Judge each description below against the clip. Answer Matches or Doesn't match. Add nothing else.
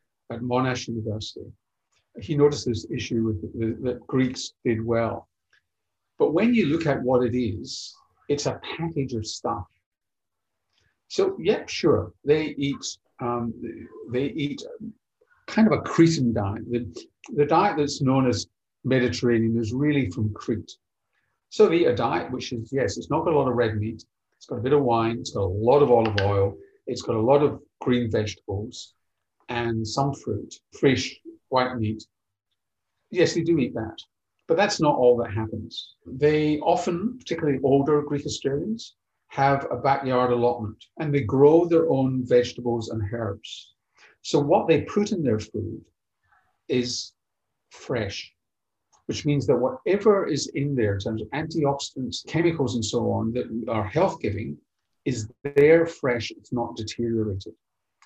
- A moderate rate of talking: Matches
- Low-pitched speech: Matches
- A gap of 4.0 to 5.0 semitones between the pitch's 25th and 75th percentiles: Matches